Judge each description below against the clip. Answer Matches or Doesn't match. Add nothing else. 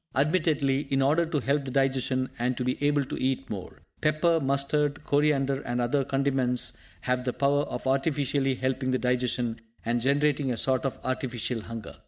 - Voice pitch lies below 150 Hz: Matches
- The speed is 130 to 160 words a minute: Doesn't match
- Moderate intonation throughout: Doesn't match